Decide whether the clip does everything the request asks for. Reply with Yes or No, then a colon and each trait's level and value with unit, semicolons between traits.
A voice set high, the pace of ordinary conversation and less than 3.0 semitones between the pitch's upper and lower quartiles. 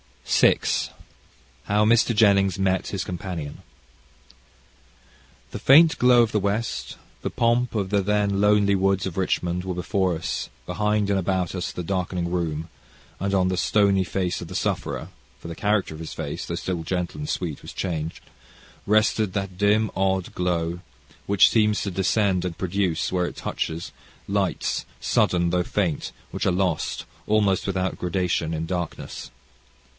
No: very low, 95 Hz; average, 160 wpm; narrow, 2.6 semitones